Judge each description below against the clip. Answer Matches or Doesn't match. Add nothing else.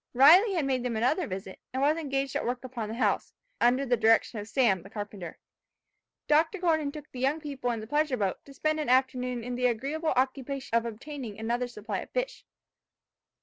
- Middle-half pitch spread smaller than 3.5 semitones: Doesn't match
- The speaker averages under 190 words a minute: Doesn't match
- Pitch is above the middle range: Matches